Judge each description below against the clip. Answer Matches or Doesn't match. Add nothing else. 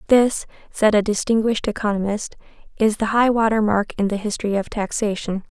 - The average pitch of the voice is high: Matches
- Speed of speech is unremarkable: Matches